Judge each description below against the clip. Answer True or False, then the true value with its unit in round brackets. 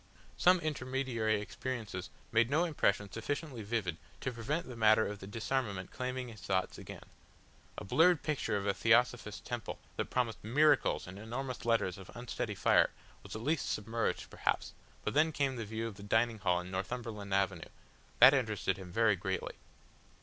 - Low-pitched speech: True (115 Hz)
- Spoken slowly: False (165 wpm)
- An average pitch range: True (4.1 semitones)